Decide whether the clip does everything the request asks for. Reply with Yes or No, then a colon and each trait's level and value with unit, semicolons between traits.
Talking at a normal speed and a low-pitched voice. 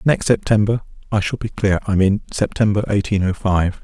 Yes: average, 190 wpm; low, 100 Hz